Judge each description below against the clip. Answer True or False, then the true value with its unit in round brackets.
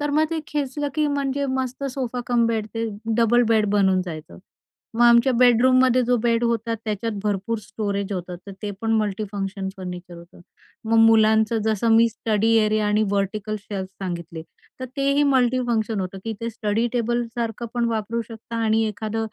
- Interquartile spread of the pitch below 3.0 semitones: True (2.6 semitones)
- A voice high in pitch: True (225 Hz)